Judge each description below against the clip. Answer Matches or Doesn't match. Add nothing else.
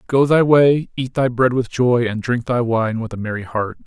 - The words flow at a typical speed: Doesn't match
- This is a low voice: Matches